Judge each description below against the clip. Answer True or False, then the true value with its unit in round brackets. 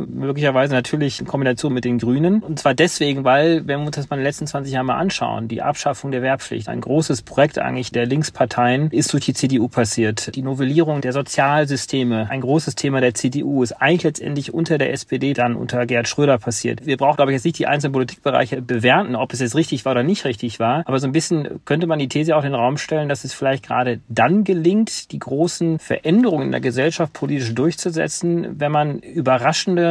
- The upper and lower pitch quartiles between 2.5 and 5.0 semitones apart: True (3.4 semitones)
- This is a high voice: False (140 Hz)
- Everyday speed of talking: False (215 wpm)